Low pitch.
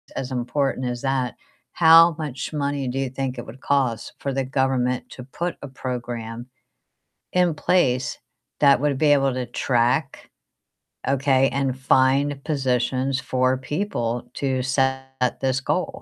Yes: low, 130 Hz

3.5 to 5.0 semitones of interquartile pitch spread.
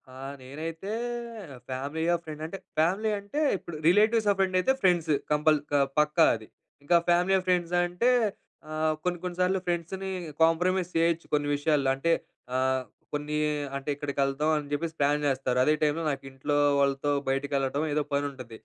Yes: average, 3.8 semitones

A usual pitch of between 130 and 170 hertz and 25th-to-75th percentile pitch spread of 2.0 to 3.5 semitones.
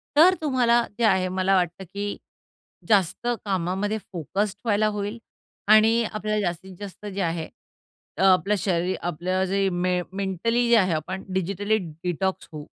No: high, 195 Hz; average, 2.8 semitones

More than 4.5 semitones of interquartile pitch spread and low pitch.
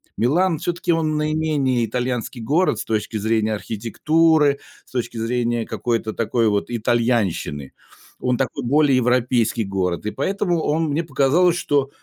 Yes: average, 5.2 semitones; low, 125 Hz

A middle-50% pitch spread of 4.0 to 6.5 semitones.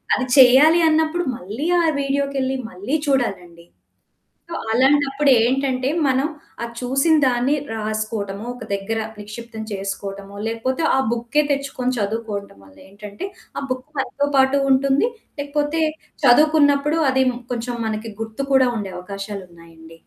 Yes: average, 5.1 semitones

